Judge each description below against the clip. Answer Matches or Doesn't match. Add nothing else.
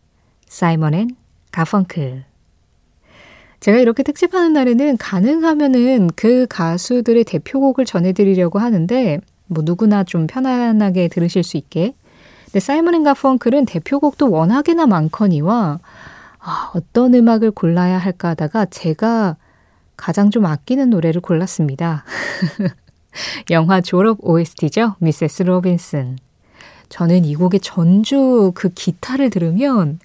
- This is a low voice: Doesn't match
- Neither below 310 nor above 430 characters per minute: Doesn't match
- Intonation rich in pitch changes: Matches